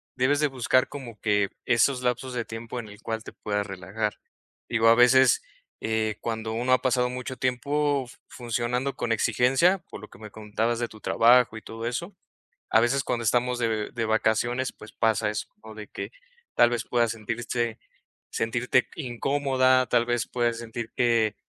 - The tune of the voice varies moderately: No, narrow, 2.2 semitones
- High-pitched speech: No, low, 120 Hz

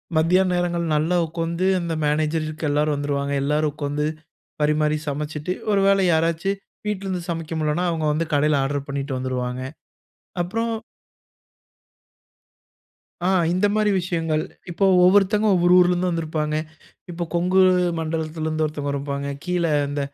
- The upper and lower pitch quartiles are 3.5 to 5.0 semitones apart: No, average, 2.9 semitones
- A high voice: No, medium, 160 Hz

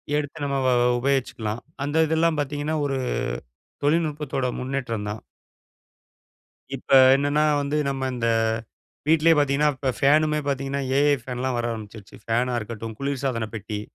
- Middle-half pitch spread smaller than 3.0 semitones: No, average, 3.5 semitones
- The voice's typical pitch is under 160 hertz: Yes, low, 135 Hz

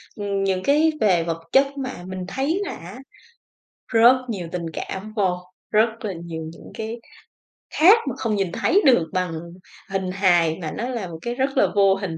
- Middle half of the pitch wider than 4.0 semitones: Yes, average, 5.3 semitones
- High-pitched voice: Yes, high, 195 Hz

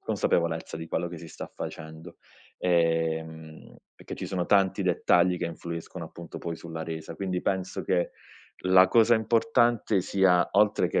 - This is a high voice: No, very low, 85 Hz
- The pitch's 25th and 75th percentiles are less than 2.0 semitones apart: No, narrow, 2.6 semitones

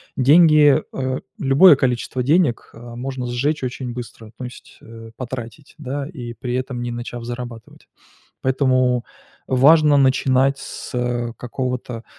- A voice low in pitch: Yes, low, 130 Hz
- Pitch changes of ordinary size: No, narrow, 2.2 semitones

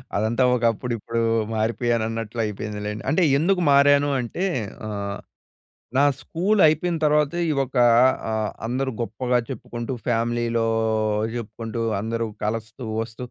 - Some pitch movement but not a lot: Yes, average, 3.8 semitones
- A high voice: No, low, 120 Hz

